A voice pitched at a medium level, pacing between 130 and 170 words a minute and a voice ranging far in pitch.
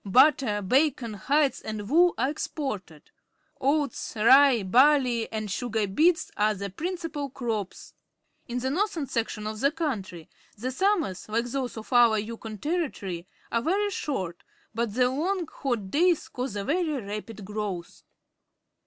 No: high, 245 Hz; average, 145 wpm; wide, 5.9 semitones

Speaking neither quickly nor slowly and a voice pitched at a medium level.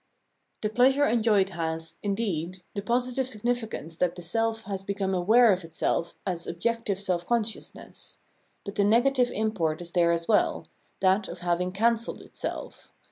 No: average, 160 wpm; high, 200 Hz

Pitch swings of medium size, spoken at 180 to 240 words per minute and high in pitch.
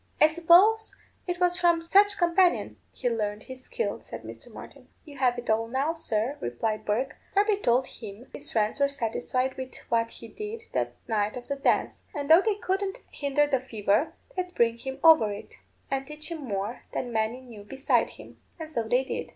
No: wide, 6.6 semitones; average, 200 wpm; very high, 265 Hz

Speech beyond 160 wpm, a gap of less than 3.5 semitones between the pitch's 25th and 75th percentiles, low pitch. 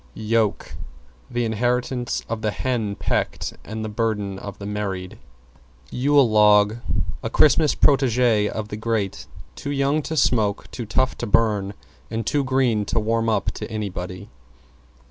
No: average, 145 wpm; average, 3.0 semitones; low, 110 Hz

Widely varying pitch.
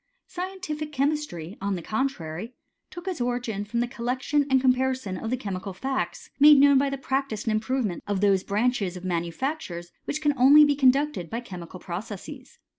Yes: wide, 6.1 semitones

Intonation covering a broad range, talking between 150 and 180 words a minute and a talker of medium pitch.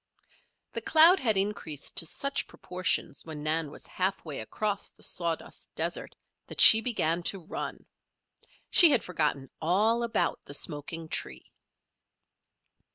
No: wide, 5.7 semitones; slow, 135 wpm; medium, 180 Hz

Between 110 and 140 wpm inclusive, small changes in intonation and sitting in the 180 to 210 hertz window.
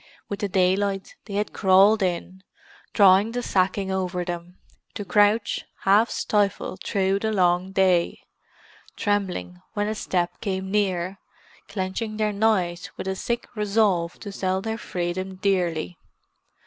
Yes: slow, 135 wpm; narrow, 2.1 semitones; high, 190 Hz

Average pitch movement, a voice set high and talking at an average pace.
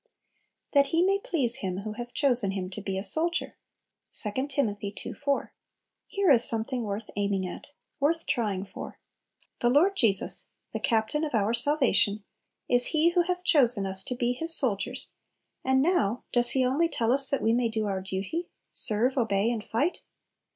No: wide, 5.7 semitones; high, 240 Hz; average, 180 wpm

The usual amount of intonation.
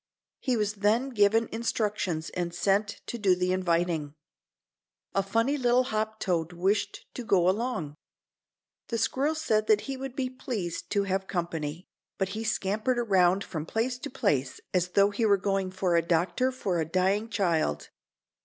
Yes: average, 4.1 semitones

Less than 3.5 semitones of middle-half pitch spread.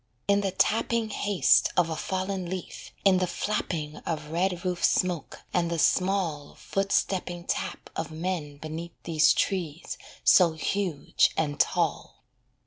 Yes: average, 3.1 semitones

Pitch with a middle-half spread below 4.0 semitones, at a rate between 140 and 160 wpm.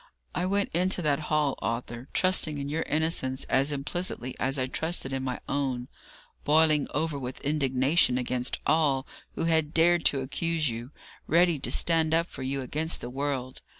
No: average, 3.6 semitones; average, 170 wpm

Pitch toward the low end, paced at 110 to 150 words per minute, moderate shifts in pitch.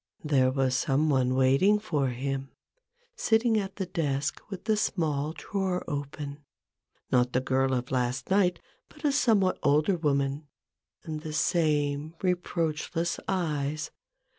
No: medium, 150 Hz; average, 140 wpm; average, 4.8 semitones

